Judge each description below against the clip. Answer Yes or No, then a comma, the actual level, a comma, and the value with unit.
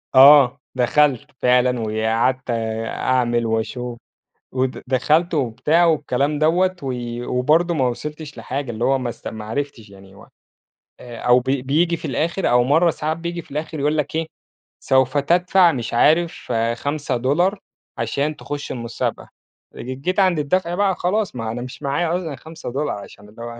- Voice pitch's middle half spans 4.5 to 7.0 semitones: Yes, average, 4.8 semitones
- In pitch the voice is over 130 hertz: Yes, medium, 140 Hz